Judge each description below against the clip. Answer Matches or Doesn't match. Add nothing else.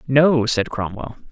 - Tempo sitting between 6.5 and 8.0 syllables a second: Doesn't match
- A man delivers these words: Matches